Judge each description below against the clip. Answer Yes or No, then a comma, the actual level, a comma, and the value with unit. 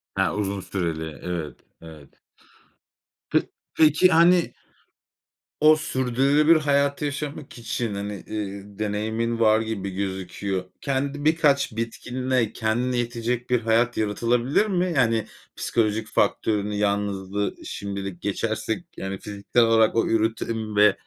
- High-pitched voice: No, low, 110 Hz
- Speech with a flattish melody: No, average, 4.2 semitones